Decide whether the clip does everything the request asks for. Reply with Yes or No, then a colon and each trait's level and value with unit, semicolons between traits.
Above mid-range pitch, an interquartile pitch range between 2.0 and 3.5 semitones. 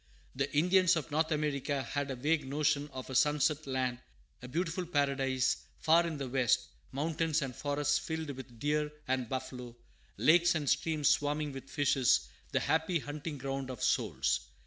No: medium, 145 Hz; average, 2.9 semitones